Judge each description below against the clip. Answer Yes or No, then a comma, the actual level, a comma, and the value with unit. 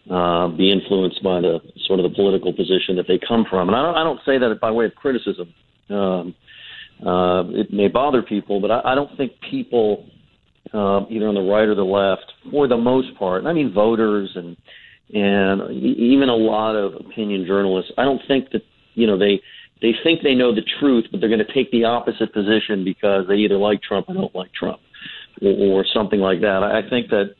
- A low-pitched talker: Yes, low, 100 Hz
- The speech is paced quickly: Yes, fast, 220 wpm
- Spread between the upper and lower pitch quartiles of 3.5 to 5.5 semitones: No, average, 3.0 semitones